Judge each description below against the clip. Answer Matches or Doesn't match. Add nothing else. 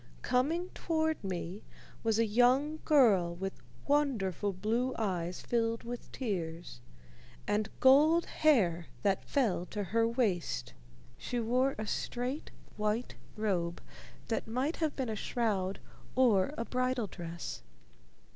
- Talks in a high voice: Matches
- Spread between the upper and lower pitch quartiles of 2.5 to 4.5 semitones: Doesn't match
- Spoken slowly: Matches